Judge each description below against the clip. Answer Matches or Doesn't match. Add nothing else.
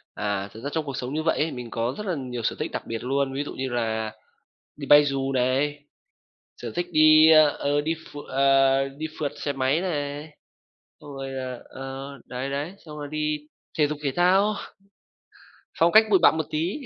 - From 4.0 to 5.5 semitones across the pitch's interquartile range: Doesn't match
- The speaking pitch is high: Doesn't match